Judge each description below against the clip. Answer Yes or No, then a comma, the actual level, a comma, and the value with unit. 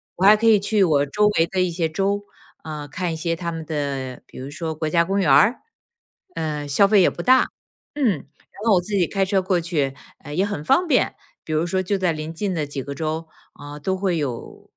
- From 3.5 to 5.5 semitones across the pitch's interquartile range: Yes, average, 4.5 semitones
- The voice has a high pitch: No, medium, 170 Hz